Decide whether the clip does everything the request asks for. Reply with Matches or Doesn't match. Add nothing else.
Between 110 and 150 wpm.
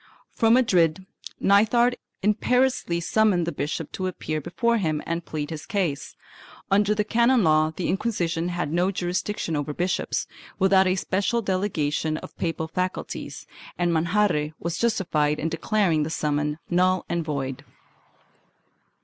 Matches